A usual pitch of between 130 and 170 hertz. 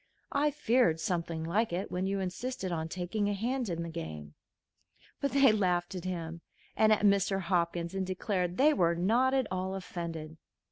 No: medium, 185 Hz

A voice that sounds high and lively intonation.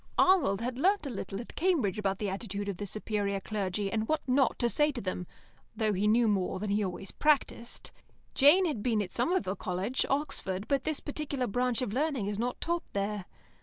Yes: high, 220 Hz; wide, 5.7 semitones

